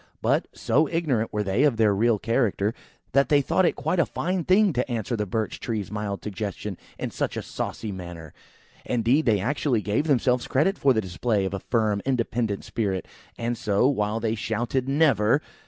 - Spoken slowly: No, average, 190 wpm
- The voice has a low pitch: Yes, low, 115 Hz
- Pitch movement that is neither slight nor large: Yes, average, 4.5 semitones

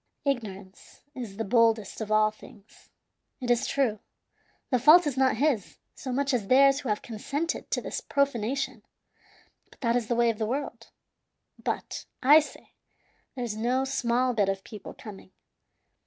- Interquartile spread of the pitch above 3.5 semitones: Yes, average, 3.9 semitones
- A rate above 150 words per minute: Yes, average, 160 wpm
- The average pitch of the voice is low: No, high, 240 Hz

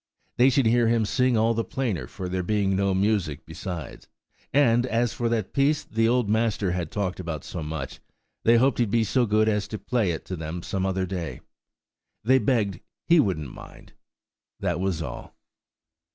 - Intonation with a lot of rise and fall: No, average, 4.5 semitones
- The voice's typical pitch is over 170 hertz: No, low, 105 Hz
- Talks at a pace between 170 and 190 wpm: Yes, average, 180 wpm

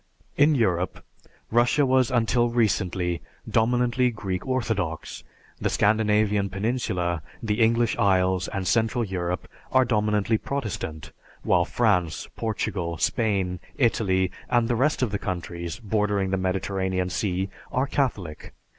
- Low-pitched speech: Yes, low, 105 Hz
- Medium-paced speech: No, slow, 120 wpm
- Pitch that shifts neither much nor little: Yes, average, 4.4 semitones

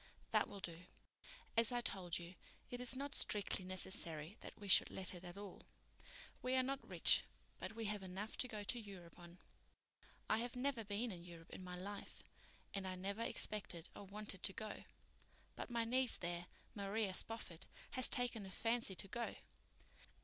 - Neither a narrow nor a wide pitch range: Yes, average, 4.1 semitones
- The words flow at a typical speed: Yes, average, 180 wpm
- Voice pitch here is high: Yes, high, 205 Hz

